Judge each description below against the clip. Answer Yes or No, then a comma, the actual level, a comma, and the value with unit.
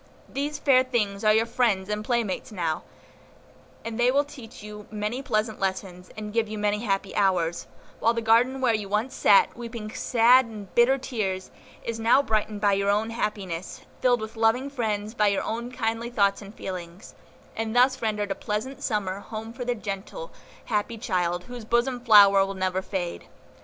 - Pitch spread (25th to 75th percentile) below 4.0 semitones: Yes, average, 3.1 semitones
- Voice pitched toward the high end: Yes, high, 215 Hz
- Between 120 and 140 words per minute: No, average, 180 wpm